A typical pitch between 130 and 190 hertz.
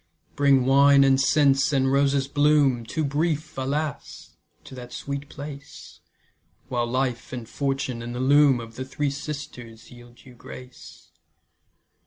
Yes: low, 135 Hz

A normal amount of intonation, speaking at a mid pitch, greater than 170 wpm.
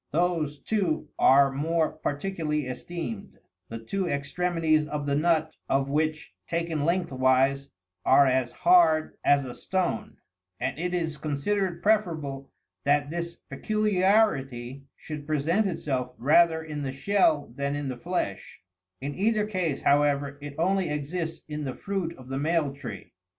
No: average, 3.8 semitones; medium, 155 Hz; average, 145 wpm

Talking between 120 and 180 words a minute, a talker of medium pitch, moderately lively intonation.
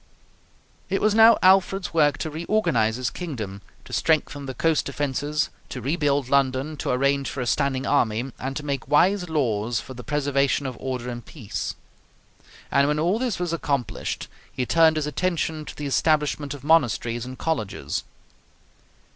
Yes: average, 165 wpm; medium, 145 Hz; average, 3.7 semitones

